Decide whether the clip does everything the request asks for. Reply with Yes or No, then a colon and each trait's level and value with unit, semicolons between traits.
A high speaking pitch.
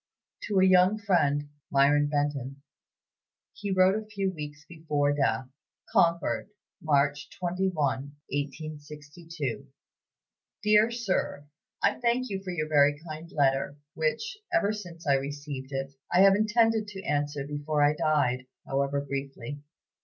No: medium, 150 Hz